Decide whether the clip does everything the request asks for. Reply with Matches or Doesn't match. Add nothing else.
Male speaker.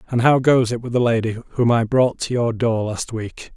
Matches